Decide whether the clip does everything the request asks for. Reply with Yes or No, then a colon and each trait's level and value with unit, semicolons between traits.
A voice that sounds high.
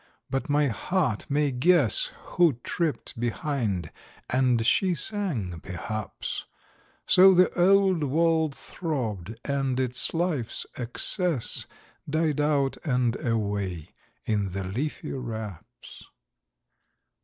No: low, 135 Hz